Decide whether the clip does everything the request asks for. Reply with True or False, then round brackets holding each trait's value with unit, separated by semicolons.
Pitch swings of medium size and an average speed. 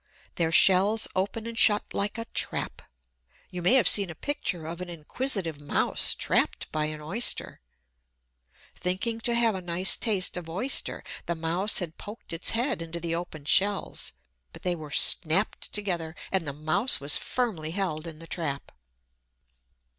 True (4.3 semitones; 160 wpm)